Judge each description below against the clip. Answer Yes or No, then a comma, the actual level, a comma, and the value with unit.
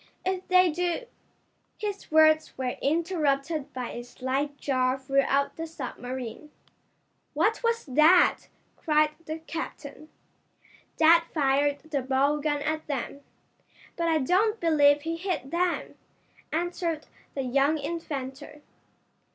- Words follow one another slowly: Yes, slow, 120 wpm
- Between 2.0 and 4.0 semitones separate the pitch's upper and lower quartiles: Yes, average, 3.4 semitones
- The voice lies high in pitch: Yes, very high, 305 Hz